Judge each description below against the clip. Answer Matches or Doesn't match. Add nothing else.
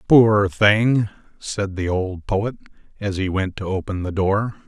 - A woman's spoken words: Doesn't match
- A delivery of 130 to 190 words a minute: Matches